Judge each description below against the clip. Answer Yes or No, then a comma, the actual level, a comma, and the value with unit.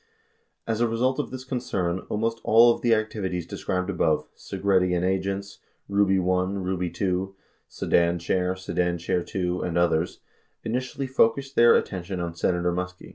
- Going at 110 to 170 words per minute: Yes, average, 165 wpm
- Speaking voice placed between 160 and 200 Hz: No, very low, 95 Hz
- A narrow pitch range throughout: No, average, 4.0 semitones